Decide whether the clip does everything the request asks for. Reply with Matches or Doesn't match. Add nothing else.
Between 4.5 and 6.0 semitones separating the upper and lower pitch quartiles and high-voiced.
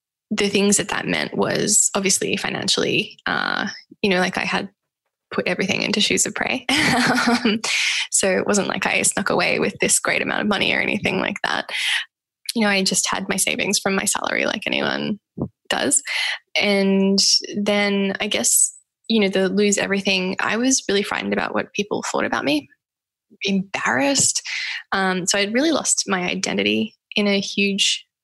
Doesn't match